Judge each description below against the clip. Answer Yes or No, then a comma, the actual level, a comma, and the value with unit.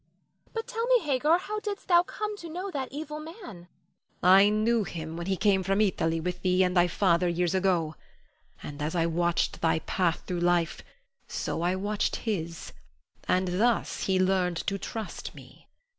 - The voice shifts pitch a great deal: Yes, wide, 6.9 semitones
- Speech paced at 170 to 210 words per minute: Yes, average, 180 wpm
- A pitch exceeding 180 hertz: Yes, high, 190 Hz